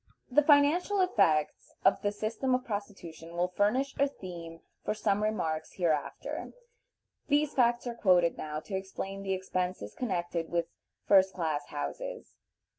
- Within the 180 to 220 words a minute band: No, average, 140 wpm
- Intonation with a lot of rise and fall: Yes, wide, 6.4 semitones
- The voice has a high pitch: Yes, high, 195 Hz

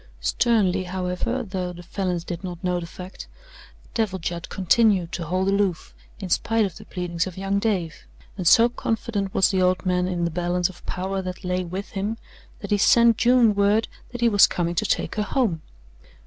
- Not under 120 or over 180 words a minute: No, average, 195 wpm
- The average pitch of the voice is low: No, high, 190 Hz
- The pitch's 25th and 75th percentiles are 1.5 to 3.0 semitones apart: Yes, narrow, 2.6 semitones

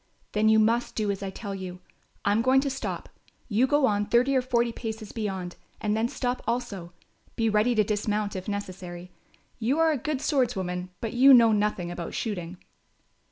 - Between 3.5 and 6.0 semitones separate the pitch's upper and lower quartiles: Yes, average, 3.8 semitones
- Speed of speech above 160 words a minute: Yes, average, 190 wpm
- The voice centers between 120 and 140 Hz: No, high, 215 Hz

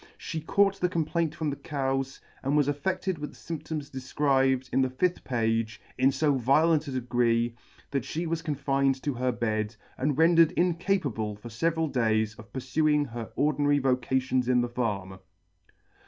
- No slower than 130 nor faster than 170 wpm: Yes, average, 165 wpm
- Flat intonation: No, average, 4.1 semitones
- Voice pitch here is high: No, low, 135 Hz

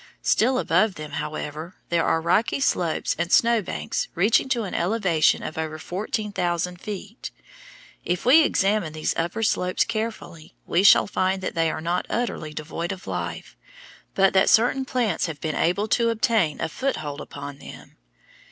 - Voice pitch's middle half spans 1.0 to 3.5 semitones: No, average, 5.1 semitones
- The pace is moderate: Yes, average, 165 wpm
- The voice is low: No, medium, 185 Hz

